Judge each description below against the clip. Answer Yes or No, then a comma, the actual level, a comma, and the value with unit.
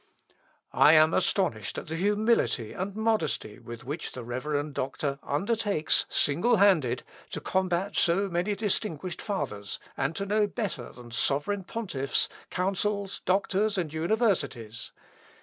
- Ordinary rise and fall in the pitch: No, wide, 6.5 semitones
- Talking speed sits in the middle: No, slow, 130 wpm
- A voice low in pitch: No, medium, 175 Hz